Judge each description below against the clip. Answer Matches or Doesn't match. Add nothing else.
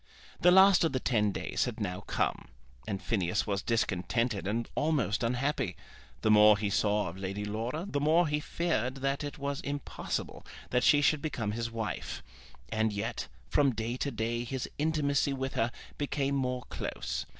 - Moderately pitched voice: Doesn't match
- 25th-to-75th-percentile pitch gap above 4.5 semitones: Matches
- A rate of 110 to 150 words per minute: Doesn't match